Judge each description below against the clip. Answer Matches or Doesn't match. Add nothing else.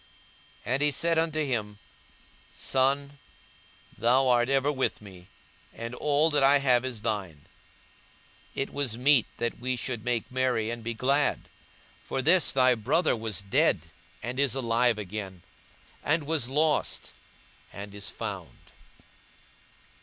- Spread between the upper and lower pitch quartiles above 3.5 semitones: Matches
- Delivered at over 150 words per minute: Doesn't match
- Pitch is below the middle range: Matches